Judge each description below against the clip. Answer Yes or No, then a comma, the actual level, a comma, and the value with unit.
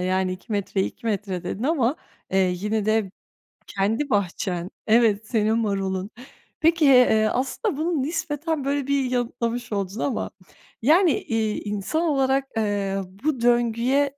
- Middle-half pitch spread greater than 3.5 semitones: Yes, average, 5.2 semitones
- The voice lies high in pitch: Yes, high, 230 Hz